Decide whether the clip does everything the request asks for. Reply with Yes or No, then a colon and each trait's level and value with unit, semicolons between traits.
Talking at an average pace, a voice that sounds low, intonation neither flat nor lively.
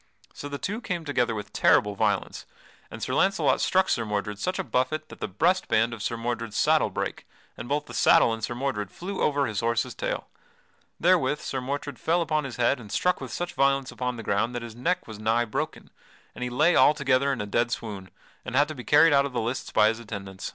No: fast, 230 wpm; low, 125 Hz; average, 4.8 semitones